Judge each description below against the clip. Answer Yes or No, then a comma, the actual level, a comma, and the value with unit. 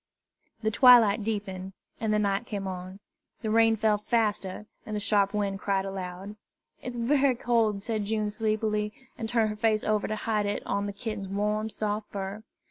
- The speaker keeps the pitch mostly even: Yes, narrow, 1.7 semitones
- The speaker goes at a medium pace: Yes, average, 180 wpm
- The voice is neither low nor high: No, high, 210 Hz